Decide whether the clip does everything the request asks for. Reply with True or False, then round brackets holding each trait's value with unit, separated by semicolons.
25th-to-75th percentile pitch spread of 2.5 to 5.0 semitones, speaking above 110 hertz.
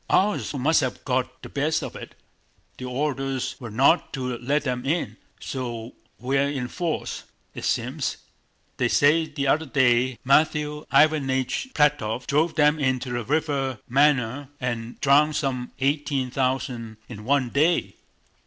True (2.9 semitones; 135 Hz)